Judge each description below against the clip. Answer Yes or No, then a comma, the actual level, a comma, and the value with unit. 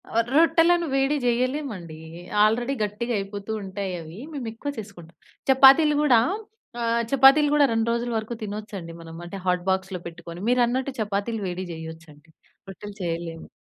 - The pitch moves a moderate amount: No, wide, 6.1 semitones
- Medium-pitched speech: No, high, 215 Hz